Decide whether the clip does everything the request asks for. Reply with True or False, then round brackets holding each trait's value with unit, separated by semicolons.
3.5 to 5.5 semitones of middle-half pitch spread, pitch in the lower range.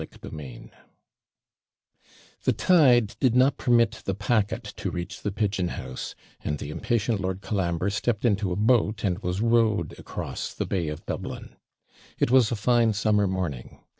True (4.2 semitones; 105 Hz)